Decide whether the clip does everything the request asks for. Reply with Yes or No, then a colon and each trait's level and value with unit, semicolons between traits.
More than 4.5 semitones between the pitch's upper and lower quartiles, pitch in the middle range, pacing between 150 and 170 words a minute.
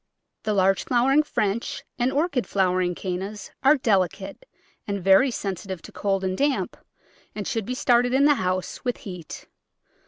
No: average, 5.1 semitones; high, 205 Hz; average, 155 wpm